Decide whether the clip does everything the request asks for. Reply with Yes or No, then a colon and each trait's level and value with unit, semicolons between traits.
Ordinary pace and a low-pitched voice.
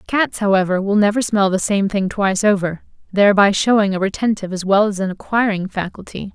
No: average, 190 wpm; high, 200 Hz